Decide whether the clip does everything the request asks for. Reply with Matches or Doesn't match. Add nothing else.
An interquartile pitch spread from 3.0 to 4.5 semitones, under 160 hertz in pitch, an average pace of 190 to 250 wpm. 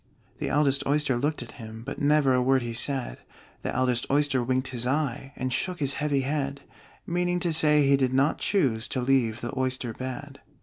Doesn't match